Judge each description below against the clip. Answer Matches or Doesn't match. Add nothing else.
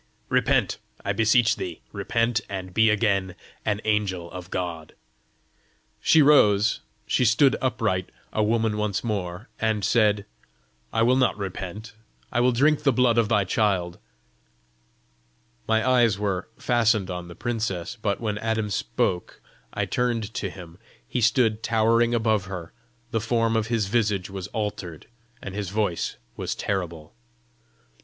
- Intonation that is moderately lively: Matches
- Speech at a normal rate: Matches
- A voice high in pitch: Doesn't match